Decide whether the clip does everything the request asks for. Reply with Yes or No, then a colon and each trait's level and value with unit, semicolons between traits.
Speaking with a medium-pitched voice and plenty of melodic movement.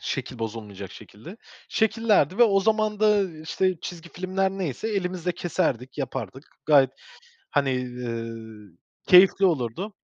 Yes: medium, 165 Hz; wide, 8.0 semitones